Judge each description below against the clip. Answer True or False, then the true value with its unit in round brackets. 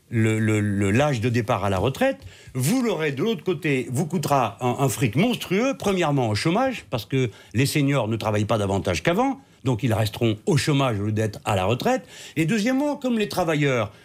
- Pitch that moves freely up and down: True (8.1 semitones)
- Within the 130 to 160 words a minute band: False (205 wpm)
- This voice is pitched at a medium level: False (130 Hz)